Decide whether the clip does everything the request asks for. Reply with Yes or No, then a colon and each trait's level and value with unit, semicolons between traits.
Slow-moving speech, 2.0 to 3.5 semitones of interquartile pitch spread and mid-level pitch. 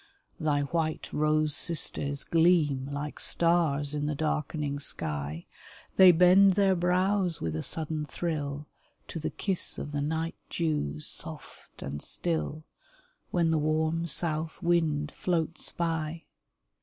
Yes: slow, 130 wpm; average, 2.7 semitones; medium, 155 Hz